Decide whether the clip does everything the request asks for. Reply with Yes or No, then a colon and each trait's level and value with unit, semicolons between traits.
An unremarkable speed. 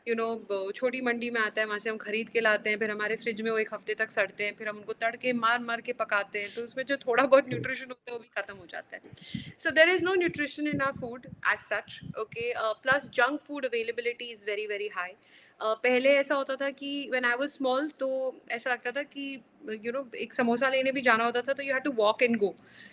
No: fast, 255 wpm